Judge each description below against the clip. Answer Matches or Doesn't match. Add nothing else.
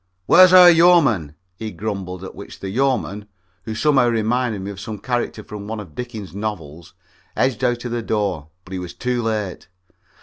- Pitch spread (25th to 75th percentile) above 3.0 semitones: Matches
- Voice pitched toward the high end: Doesn't match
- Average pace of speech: Matches